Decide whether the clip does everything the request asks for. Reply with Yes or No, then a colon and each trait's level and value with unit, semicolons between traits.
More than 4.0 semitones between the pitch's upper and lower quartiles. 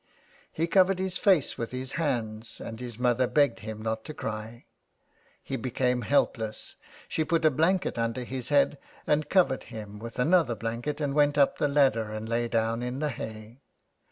Yes: average, 4.5 semitones